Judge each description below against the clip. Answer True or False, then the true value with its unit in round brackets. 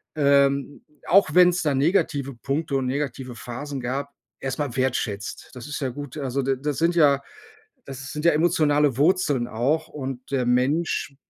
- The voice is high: False (140 Hz)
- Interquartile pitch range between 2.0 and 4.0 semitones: True (2.4 semitones)